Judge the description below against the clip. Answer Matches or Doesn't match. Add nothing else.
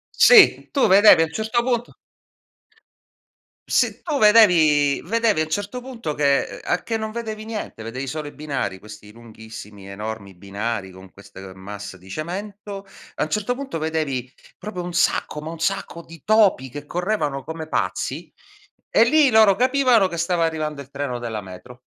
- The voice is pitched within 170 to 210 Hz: Doesn't match